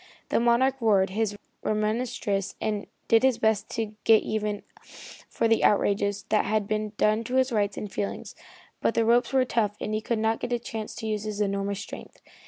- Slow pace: No, average, 200 wpm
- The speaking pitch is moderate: No, high, 215 Hz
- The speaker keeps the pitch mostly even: Yes, narrow, 1.8 semitones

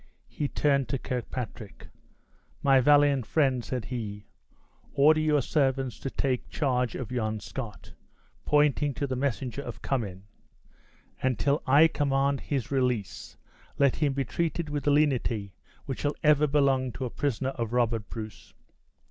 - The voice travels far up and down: No, average, 3.0 semitones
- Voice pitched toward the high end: No, low, 135 Hz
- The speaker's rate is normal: Yes, average, 150 wpm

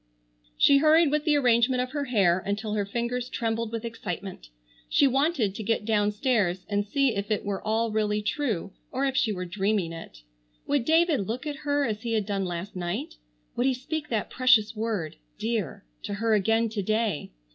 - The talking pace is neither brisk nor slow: Yes, average, 190 wpm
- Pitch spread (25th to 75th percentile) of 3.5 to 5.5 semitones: Yes, average, 4.0 semitones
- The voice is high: Yes, high, 225 Hz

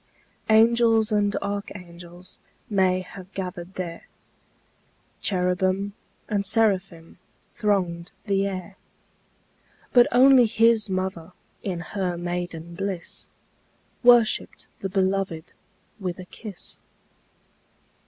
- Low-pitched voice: No, high, 190 Hz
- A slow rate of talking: Yes, slow, 90 wpm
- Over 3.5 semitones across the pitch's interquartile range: No, narrow, 2.6 semitones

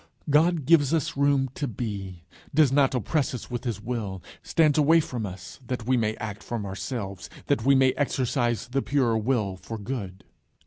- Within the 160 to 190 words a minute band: Yes, average, 180 wpm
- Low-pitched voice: Yes, low, 125 Hz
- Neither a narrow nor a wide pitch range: Yes, average, 4.7 semitones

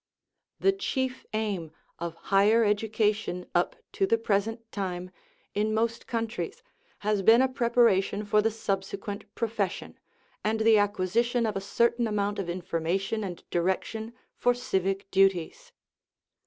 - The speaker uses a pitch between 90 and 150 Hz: No, high, 210 Hz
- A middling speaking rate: No, slow, 130 wpm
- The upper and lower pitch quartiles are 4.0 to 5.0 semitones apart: No, average, 2.9 semitones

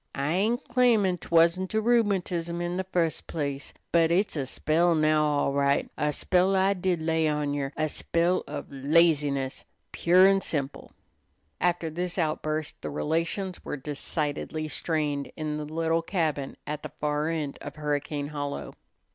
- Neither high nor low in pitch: Yes, medium, 160 Hz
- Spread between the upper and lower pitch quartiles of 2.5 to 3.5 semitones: Yes, average, 3.1 semitones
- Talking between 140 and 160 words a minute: Yes, average, 155 wpm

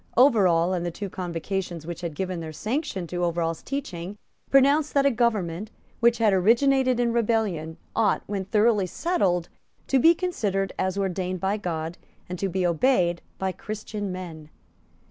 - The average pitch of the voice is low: No, high, 195 Hz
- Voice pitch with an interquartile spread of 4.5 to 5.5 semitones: Yes, average, 5.1 semitones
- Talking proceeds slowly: No, average, 160 wpm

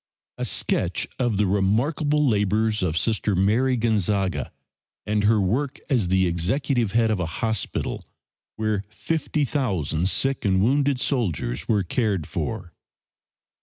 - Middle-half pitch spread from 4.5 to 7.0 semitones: Yes, average, 4.8 semitones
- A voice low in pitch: Yes, low, 105 Hz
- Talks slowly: Yes, slow, 130 wpm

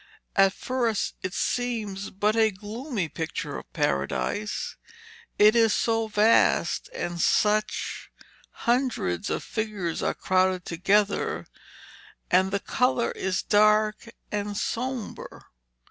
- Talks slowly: Yes, slow, 110 wpm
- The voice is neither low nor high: No, high, 210 Hz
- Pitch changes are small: No, average, 3.1 semitones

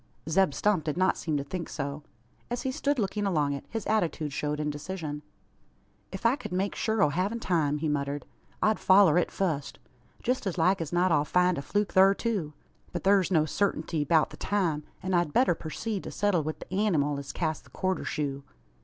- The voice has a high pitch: No, medium, 175 Hz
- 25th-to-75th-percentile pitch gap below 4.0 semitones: No, average, 4.8 semitones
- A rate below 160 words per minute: No, fast, 205 wpm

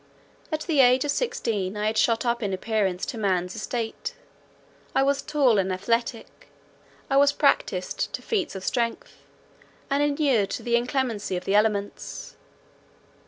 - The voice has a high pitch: Yes, high, 230 Hz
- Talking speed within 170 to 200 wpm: No, average, 155 wpm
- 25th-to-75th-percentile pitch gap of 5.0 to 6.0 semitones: Yes, average, 5.3 semitones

